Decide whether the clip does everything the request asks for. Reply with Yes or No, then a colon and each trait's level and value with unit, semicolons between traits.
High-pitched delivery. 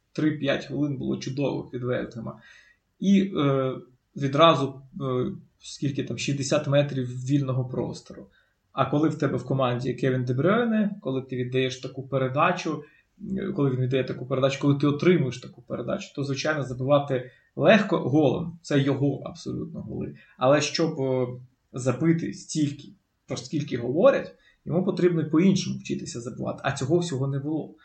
No: medium, 140 Hz